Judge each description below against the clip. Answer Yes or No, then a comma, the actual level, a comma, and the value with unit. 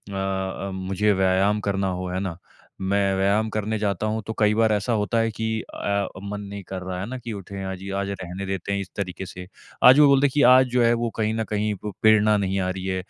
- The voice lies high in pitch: No, low, 100 Hz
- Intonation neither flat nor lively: No, narrow, 2.3 semitones